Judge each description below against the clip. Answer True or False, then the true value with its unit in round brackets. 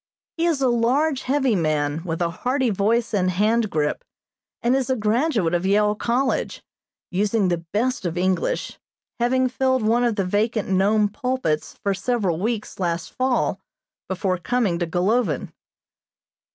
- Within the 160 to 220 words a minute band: False (150 wpm)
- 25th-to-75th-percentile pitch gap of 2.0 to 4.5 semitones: False (5.3 semitones)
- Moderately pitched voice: False (215 Hz)